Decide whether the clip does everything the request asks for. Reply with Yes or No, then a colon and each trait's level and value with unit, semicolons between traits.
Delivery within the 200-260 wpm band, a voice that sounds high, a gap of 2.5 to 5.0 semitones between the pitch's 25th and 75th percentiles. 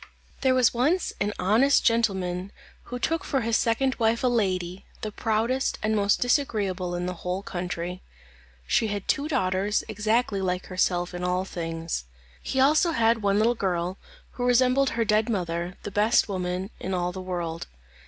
No: average, 175 wpm; high, 205 Hz; average, 4.6 semitones